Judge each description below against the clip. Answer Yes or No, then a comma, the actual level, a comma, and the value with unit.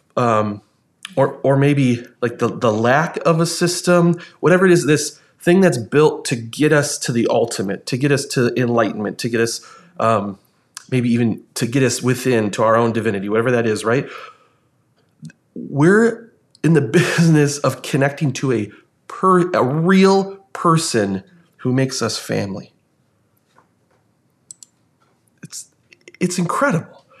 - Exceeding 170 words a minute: No, average, 145 wpm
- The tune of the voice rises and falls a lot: Yes, wide, 6.1 semitones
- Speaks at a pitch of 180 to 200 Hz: No, medium, 140 Hz